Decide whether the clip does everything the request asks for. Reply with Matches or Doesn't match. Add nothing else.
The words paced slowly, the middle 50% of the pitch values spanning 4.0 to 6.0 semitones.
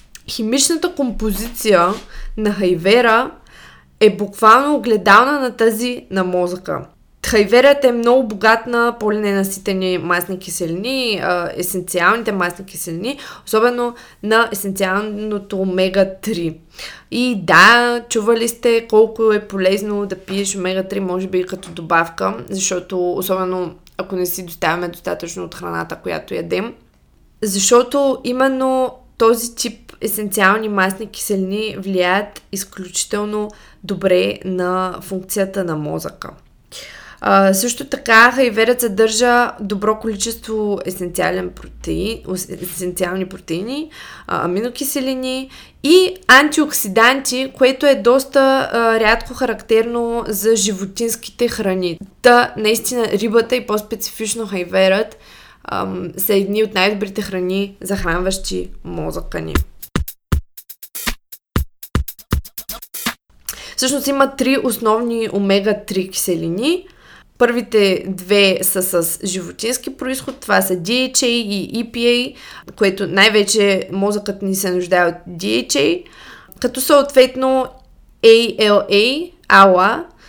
Matches